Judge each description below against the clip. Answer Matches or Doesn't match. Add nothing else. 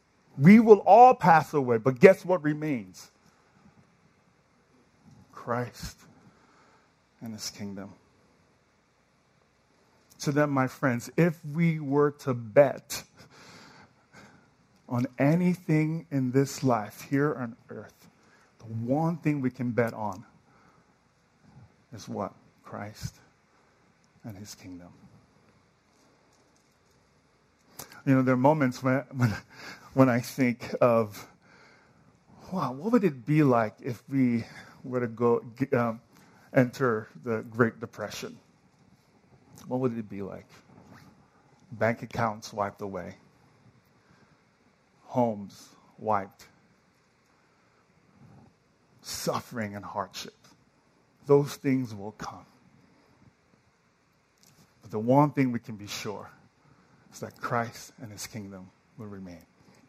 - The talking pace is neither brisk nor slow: Doesn't match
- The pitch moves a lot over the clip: Doesn't match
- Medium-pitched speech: Doesn't match